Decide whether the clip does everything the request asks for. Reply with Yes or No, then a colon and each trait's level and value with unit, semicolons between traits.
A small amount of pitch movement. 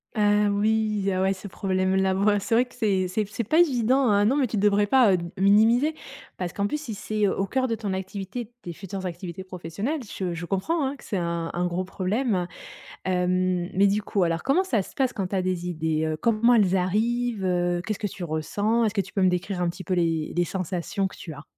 No: average, 3.3 semitones